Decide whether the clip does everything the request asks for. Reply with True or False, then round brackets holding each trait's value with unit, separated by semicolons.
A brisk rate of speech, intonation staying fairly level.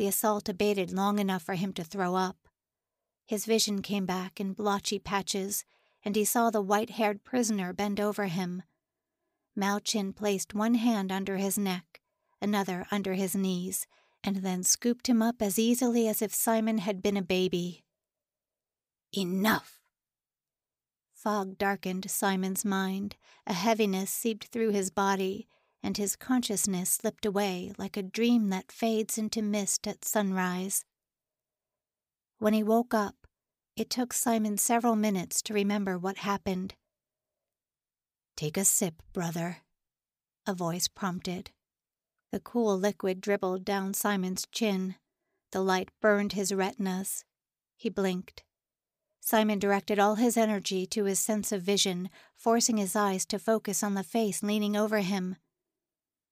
False (140 wpm; 2.2 semitones)